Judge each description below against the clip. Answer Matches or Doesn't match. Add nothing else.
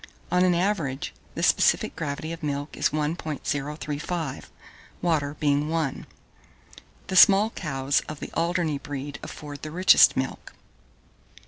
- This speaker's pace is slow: Matches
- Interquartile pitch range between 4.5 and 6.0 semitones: Doesn't match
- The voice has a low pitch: Doesn't match